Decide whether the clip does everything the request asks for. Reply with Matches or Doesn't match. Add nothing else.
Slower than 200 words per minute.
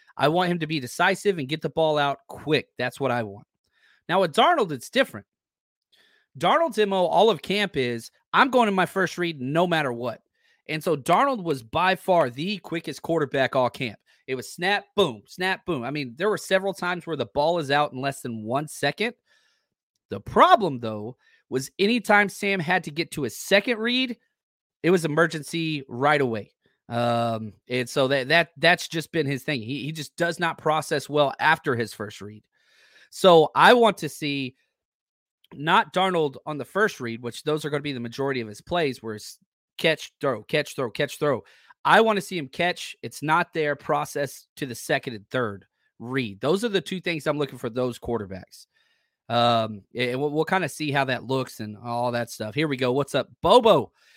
Doesn't match